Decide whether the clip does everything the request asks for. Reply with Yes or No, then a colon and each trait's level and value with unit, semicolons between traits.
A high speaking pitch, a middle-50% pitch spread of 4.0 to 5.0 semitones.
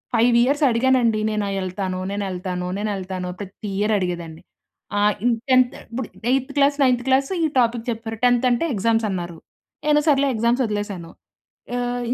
Yes: high, 230 Hz; average, 4.5 semitones